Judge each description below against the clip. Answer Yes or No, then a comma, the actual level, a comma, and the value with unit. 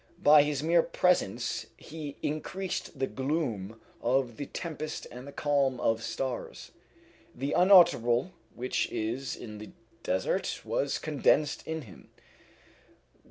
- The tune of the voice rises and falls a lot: No, average, 4.5 semitones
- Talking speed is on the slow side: Yes, slow, 120 wpm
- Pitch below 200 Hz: Yes, medium, 140 Hz